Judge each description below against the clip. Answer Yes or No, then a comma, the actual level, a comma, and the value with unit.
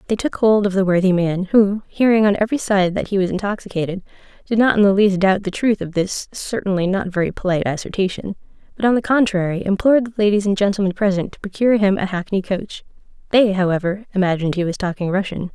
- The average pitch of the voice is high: Yes, high, 195 Hz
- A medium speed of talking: No, fast, 210 wpm